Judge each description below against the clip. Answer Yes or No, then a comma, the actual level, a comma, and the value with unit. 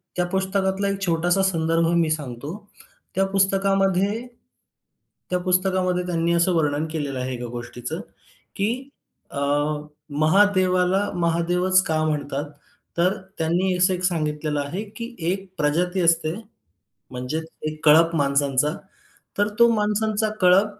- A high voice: No, medium, 180 Hz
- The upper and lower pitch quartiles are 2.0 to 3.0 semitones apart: No, average, 3.7 semitones